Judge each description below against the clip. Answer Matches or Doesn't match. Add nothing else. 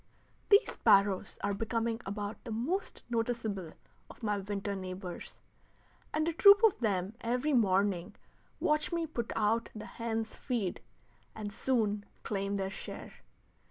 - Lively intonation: Doesn't match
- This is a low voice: Doesn't match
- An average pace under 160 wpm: Matches